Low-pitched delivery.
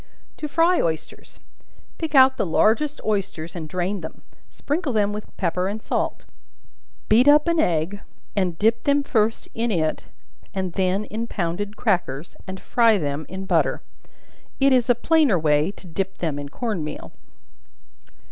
No: high, 200 Hz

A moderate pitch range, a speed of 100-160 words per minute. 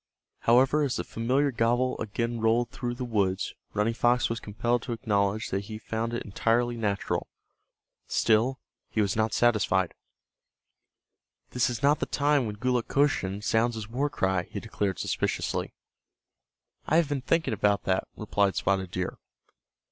Yes: average, 3.2 semitones; average, 150 wpm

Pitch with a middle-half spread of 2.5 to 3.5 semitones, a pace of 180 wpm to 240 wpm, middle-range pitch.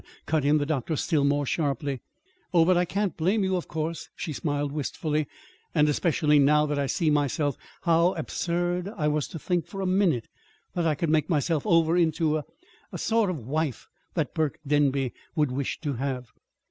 Yes: average, 2.9 semitones; average, 195 wpm; medium, 155 Hz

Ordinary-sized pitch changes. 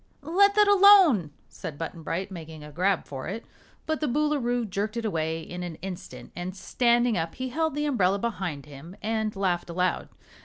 No: wide, 7.0 semitones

